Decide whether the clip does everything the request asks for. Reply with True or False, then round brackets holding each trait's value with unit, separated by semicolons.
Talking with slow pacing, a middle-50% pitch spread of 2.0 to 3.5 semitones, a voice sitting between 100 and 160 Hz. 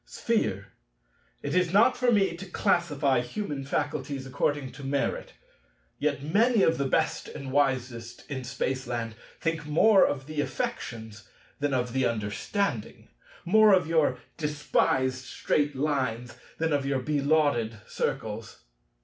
False (130 wpm; 4.0 semitones; 140 Hz)